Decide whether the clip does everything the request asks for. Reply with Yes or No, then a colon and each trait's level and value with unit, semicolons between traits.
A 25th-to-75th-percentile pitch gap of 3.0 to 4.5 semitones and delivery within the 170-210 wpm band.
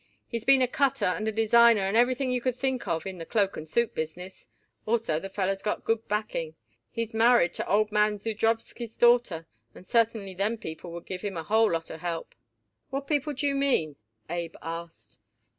No: average, 5.3 semitones; average, 195 wpm